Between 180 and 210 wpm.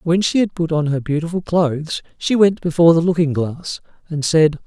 Yes: fast, 205 wpm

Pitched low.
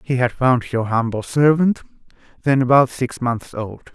Yes: low, 125 Hz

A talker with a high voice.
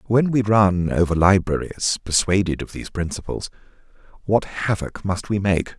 No: very low, 95 Hz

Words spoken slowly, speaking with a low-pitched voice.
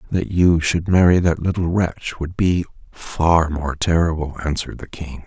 No: average, 170 wpm; very low, 85 Hz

